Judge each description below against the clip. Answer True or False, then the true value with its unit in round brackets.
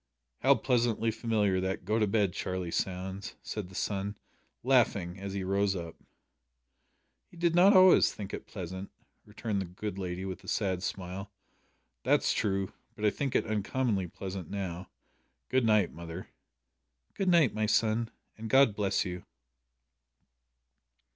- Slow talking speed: False (150 wpm)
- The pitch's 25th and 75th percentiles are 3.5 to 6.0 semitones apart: False (3.1 semitones)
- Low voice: True (100 Hz)